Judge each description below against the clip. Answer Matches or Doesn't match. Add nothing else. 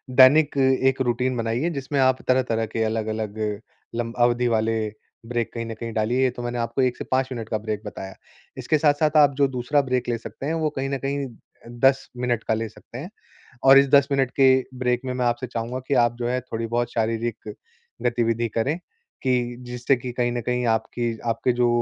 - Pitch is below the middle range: Matches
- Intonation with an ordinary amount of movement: Doesn't match